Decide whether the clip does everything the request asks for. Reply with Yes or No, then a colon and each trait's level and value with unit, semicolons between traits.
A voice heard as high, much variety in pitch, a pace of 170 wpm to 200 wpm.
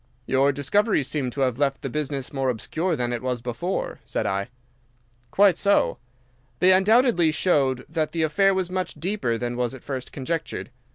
No: medium, 145 Hz; wide, 6.1 semitones; average, 175 wpm